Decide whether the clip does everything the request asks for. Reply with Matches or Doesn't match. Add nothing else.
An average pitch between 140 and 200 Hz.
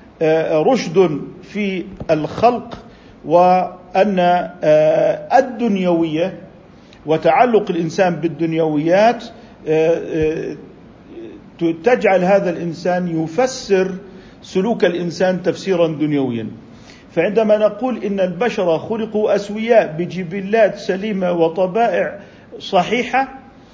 Matches